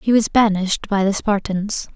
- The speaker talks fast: No, average, 185 wpm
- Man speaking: No, female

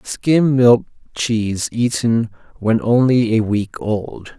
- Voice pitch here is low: Yes, low, 115 Hz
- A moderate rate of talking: No, slow, 125 wpm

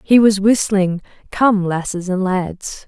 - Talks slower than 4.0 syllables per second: Yes, 3.6 syllables/s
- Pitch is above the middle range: Yes, high, 195 Hz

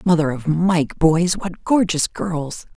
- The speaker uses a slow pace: Yes, slow, 130 wpm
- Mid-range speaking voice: Yes, medium, 170 Hz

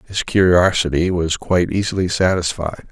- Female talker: No, male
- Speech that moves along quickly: No, slow, 125 wpm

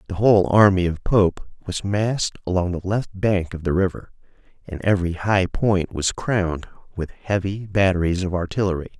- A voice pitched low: Yes, very low, 95 Hz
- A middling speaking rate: Yes, average, 165 wpm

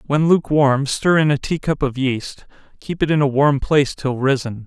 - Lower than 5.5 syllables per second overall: Yes, 5.0 syllables/s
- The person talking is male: Yes, male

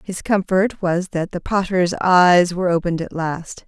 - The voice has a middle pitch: Yes, medium, 180 Hz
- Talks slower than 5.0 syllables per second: Yes, 4.6 syllables/s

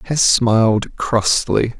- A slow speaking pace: Yes, slow, 100 wpm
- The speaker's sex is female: No, male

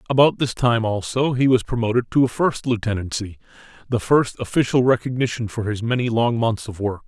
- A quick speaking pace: No, average, 185 wpm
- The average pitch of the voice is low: Yes, low, 115 Hz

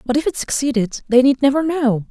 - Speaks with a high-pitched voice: Yes, very high, 265 Hz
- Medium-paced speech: No, fast, 230 wpm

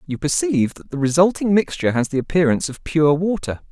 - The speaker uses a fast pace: No, average, 195 wpm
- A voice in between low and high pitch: Yes, medium, 150 Hz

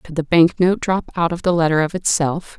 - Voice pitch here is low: No, medium, 170 Hz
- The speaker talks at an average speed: No, fast, 255 wpm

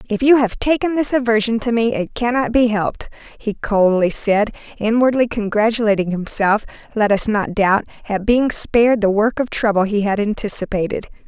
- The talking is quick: No, average, 170 wpm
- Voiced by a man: No, female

